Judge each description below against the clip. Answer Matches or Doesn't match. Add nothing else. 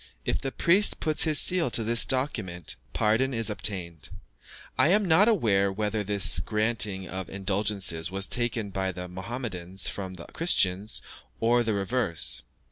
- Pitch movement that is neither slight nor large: Matches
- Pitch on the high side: Doesn't match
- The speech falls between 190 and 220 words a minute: Doesn't match